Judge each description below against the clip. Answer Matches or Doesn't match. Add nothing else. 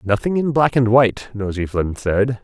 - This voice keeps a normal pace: Matches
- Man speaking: Matches